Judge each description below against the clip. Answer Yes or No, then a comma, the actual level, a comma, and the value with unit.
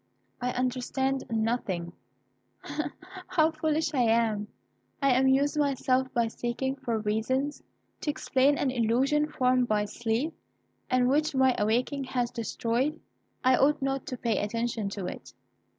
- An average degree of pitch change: Yes, average, 3.1 semitones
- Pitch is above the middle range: Yes, very high, 255 Hz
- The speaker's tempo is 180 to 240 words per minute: No, slow, 135 wpm